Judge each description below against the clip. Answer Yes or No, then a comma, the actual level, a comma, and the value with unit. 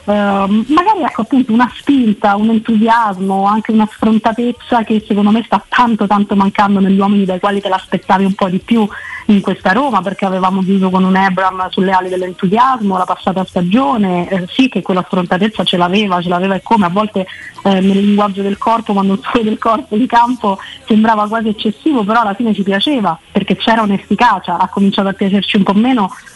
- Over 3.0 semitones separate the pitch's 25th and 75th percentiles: No, average, 2.7 semitones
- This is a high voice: Yes, high, 205 Hz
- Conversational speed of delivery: No, fast, 195 wpm